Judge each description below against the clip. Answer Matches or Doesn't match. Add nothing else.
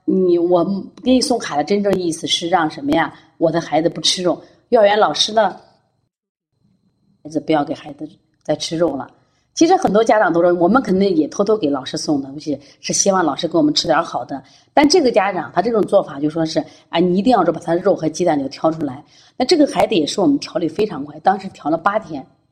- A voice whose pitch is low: Doesn't match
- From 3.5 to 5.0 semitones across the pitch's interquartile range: Matches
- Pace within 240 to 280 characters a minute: Doesn't match